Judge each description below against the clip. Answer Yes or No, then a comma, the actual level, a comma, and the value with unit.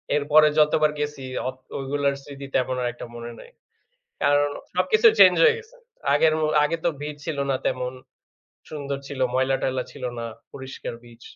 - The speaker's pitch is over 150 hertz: No, medium, 140 Hz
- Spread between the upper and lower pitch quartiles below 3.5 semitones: Yes, narrow, 2.6 semitones